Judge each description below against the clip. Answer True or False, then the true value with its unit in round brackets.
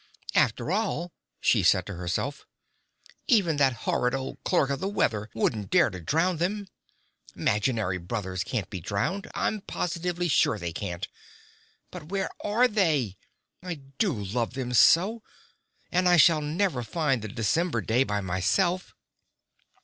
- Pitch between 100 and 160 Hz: True (135 Hz)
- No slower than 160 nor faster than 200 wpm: False (145 wpm)